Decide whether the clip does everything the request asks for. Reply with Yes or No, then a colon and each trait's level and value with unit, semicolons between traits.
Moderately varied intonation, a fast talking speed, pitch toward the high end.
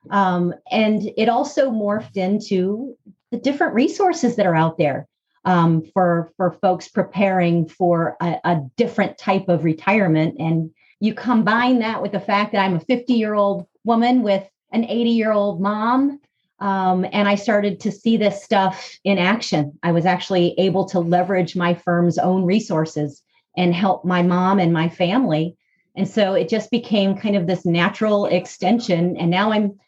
No: average, 3.4 semitones; average, 170 wpm; high, 195 Hz